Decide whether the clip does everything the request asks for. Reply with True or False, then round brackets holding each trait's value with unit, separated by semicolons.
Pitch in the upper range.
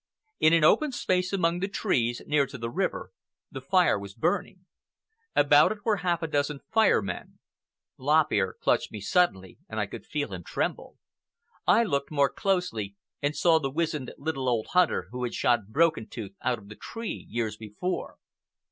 False (145 Hz)